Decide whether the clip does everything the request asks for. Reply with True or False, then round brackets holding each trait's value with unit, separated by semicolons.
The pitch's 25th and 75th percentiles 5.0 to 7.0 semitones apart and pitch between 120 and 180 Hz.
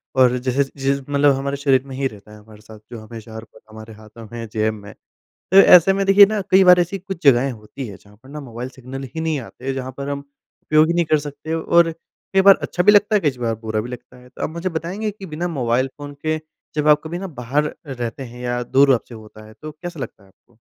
True (5.5 semitones; 135 Hz)